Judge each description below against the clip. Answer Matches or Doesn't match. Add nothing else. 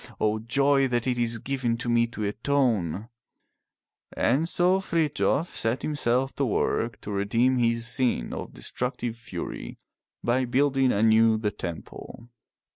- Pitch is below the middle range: Matches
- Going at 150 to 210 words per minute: Doesn't match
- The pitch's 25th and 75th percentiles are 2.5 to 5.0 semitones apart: Matches